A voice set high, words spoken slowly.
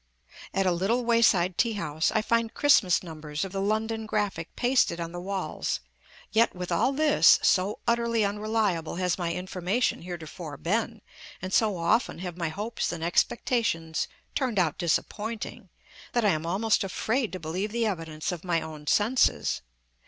No: high, 195 Hz; average, 165 wpm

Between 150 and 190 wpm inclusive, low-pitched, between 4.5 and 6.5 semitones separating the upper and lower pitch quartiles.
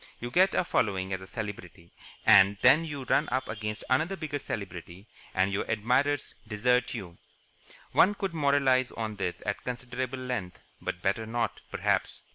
Yes: average, 160 wpm; low, 120 Hz; average, 5.1 semitones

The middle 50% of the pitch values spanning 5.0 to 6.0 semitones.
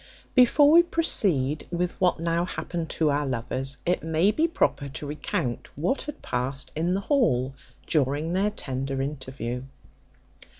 Yes: wide, 5.6 semitones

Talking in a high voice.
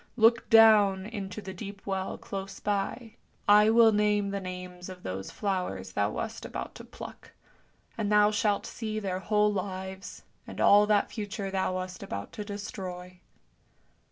Yes: high, 200 Hz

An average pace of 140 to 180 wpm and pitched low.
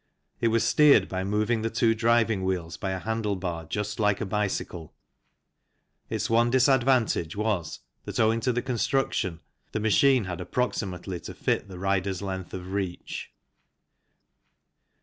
Yes: average, 145 wpm; low, 105 Hz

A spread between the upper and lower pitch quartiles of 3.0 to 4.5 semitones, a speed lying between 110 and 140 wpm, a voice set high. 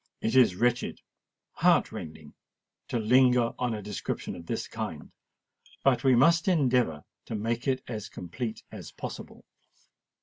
No: average, 3.3 semitones; slow, 135 wpm; low, 120 Hz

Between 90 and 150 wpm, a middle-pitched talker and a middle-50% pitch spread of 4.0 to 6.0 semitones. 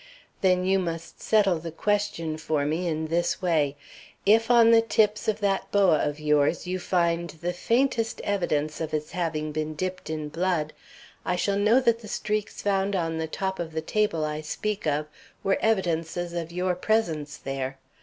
No: average, 180 wpm; medium, 175 Hz; average, 4.4 semitones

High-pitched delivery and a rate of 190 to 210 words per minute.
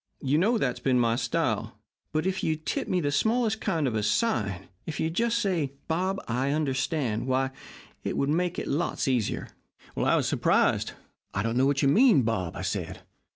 No: medium, 145 Hz; average, 195 wpm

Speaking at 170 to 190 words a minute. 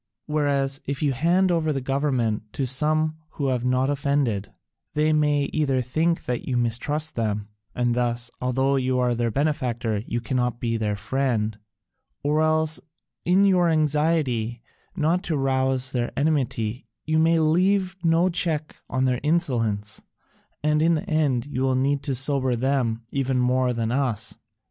No: average, 160 wpm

